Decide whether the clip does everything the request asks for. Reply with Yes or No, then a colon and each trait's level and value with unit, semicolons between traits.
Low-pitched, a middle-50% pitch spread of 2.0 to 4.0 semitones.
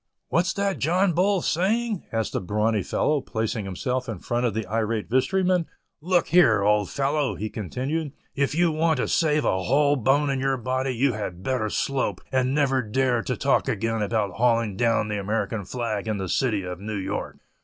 No: low, 125 Hz; wide, 5.5 semitones